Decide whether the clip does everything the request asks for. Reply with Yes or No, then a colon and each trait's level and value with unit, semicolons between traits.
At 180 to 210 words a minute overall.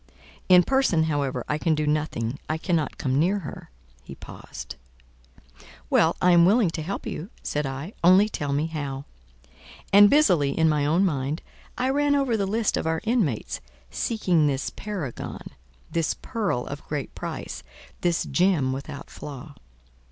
No: average, 155 wpm